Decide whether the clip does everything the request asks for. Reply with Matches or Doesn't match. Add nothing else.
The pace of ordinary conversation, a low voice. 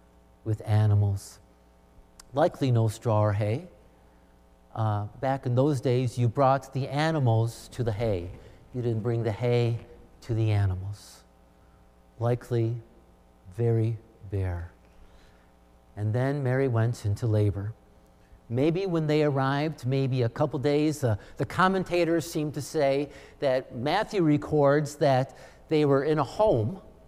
Doesn't match